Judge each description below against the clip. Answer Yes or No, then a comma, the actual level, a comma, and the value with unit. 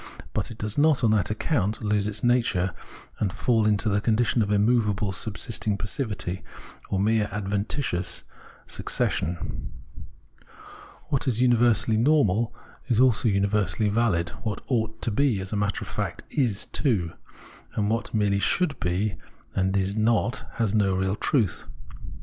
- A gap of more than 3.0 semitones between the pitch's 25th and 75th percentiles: No, average, 2.7 semitones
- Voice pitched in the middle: No, low, 105 Hz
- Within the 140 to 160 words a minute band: Yes, average, 150 wpm